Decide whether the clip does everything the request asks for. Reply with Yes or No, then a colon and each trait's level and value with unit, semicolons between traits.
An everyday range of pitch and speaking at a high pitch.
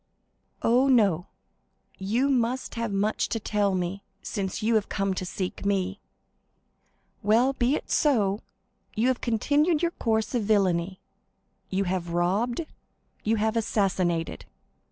Yes: average, 3.8 semitones; high, 210 Hz